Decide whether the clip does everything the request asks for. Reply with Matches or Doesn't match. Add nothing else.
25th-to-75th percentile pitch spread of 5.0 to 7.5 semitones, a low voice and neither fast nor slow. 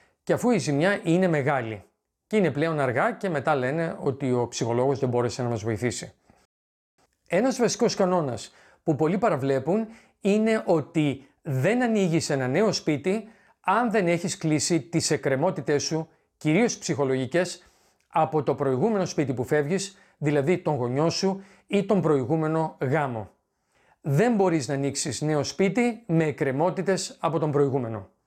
Doesn't match